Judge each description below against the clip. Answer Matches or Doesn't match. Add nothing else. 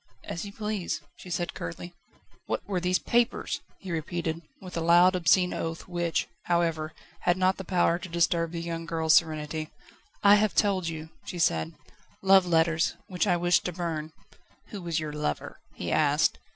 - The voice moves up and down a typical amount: Doesn't match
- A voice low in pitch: Doesn't match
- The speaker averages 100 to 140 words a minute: Doesn't match